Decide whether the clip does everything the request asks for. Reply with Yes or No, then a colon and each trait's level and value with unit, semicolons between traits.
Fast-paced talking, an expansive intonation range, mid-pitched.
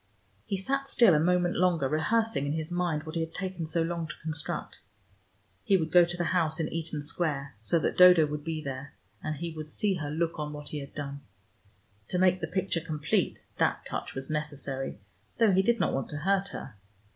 No: fast, 215 wpm; average, 3.2 semitones; medium, 160 Hz